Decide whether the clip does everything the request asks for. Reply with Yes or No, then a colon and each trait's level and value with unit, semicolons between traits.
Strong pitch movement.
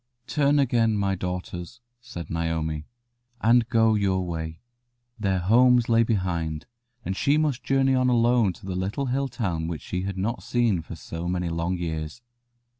Yes: wide, 5.8 semitones